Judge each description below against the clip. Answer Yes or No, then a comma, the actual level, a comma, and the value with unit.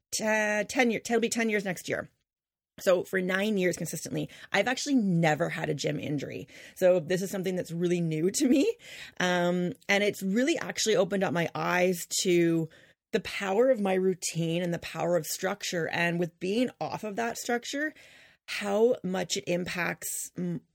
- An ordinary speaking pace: Yes, average, 180 wpm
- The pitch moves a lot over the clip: No, average, 3.8 semitones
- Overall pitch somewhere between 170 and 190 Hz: Yes, medium, 185 Hz